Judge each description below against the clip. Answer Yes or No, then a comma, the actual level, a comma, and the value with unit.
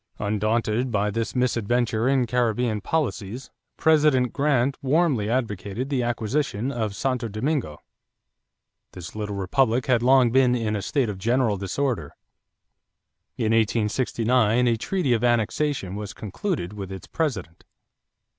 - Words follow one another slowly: Yes, slow, 125 wpm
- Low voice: Yes, low, 120 Hz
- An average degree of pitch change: Yes, average, 3.8 semitones